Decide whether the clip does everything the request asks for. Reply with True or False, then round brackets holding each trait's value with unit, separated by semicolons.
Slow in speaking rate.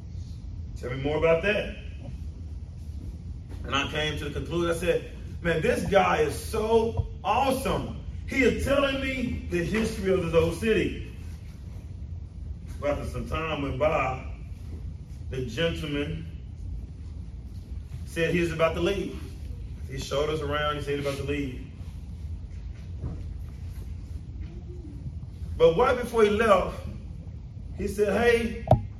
True (125 wpm)